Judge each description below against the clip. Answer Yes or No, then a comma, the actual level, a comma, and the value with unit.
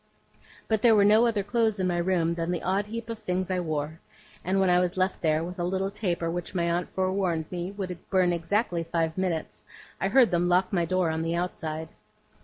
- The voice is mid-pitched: Yes, medium, 180 Hz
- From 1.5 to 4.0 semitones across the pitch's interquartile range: Yes, narrow, 2.4 semitones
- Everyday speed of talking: No, fast, 220 wpm